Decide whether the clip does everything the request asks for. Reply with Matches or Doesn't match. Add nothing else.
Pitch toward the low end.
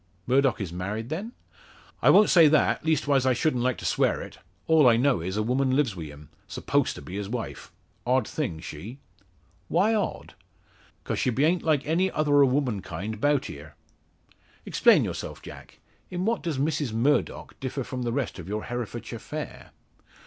Matches